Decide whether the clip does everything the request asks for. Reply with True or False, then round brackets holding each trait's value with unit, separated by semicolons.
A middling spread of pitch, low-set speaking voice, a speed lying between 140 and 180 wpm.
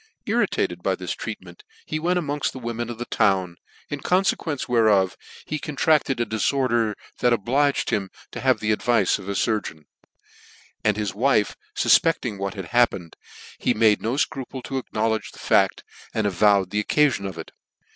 True (4.7 semitones; 115 Hz; 175 wpm)